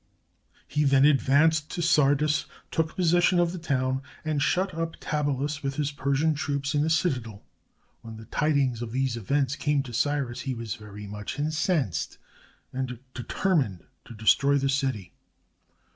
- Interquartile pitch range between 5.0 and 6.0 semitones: No, average, 3.3 semitones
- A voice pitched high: No, medium, 140 Hz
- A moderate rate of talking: Yes, average, 160 wpm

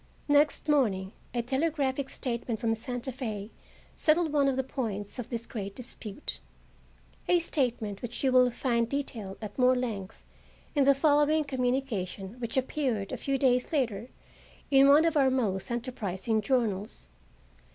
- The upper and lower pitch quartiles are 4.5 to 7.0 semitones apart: No, average, 4.0 semitones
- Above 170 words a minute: No, average, 150 wpm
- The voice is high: Yes, very high, 250 Hz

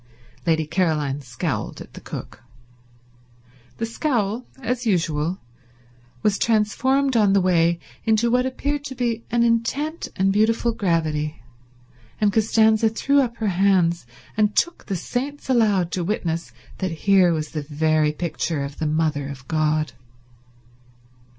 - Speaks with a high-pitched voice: Yes, high, 195 Hz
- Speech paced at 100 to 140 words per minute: Yes, slow, 135 wpm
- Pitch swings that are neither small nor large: No, wide, 6.5 semitones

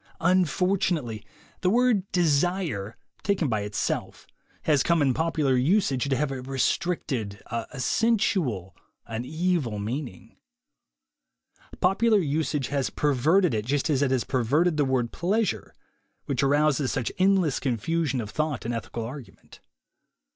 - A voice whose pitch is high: No, medium, 145 Hz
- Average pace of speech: Yes, average, 150 wpm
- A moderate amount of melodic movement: No, wide, 6.0 semitones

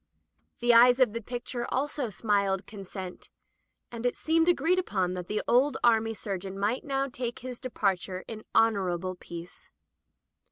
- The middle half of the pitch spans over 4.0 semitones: Yes, average, 4.5 semitones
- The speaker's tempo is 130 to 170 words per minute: Yes, average, 150 wpm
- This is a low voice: No, high, 225 Hz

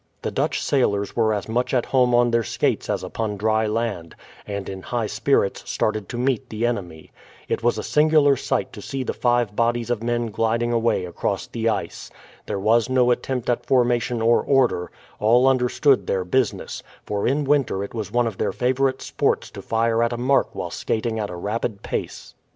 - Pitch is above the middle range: No, low, 115 Hz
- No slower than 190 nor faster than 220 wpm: Yes, average, 195 wpm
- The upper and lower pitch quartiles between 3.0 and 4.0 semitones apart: No, narrow, 2.5 semitones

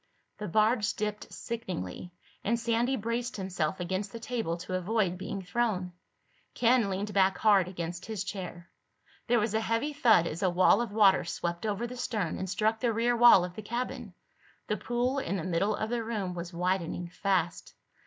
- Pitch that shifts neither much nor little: Yes, average, 4.2 semitones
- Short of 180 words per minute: No, average, 185 wpm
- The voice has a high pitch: Yes, high, 205 Hz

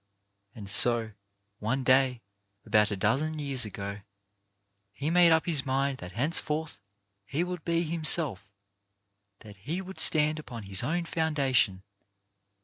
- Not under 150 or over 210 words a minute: No, average, 140 wpm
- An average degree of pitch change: No, wide, 7.1 semitones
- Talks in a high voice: No, low, 135 Hz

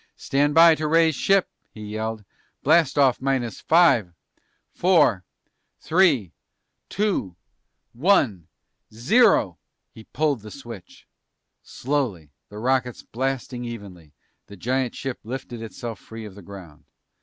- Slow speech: Yes, slow, 120 wpm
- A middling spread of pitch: No, wide, 5.7 semitones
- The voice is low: Yes, low, 120 Hz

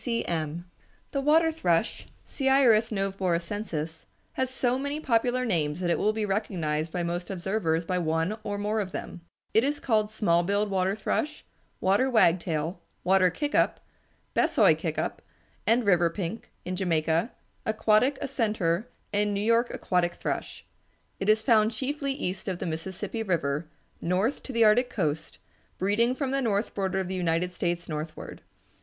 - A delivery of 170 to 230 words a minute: No, average, 160 wpm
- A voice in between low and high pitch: No, high, 200 Hz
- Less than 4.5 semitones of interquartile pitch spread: No, average, 5.0 semitones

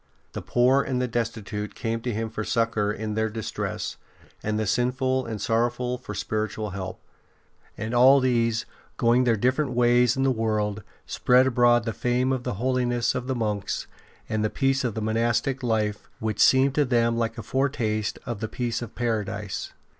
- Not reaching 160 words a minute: No, average, 175 wpm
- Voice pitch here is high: No, low, 115 Hz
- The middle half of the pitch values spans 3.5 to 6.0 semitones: No, narrow, 2.5 semitones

